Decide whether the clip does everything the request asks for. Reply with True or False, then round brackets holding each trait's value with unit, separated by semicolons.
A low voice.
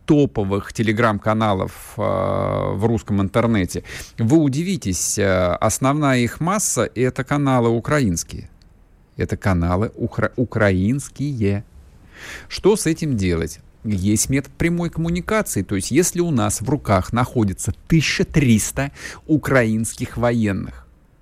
True (115 Hz)